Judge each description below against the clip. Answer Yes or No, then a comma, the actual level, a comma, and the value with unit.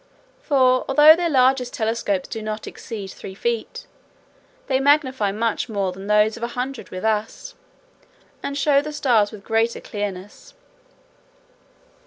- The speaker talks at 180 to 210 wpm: No, average, 140 wpm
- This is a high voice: Yes, high, 230 Hz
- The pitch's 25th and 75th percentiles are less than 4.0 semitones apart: No, average, 4.4 semitones